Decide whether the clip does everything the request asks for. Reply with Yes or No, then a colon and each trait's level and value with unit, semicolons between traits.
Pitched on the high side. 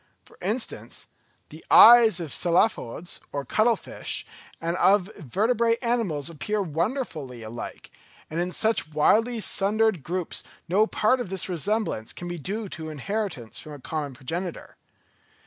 No: medium, 180 Hz